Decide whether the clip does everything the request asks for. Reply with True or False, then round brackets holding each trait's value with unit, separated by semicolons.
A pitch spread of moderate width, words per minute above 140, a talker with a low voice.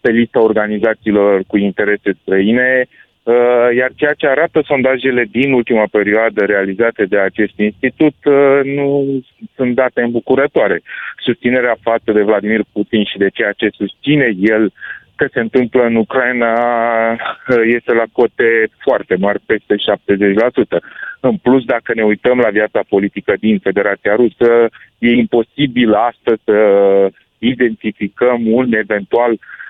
False (3.2 semitones; 125 wpm; 115 Hz)